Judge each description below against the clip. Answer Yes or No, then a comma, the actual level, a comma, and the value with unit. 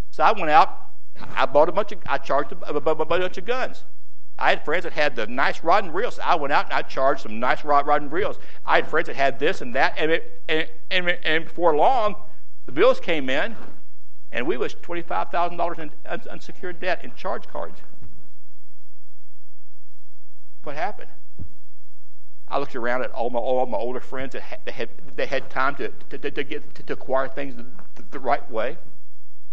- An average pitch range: No, wide, 6.3 semitones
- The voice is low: No, medium, 145 Hz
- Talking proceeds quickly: Yes, fast, 210 wpm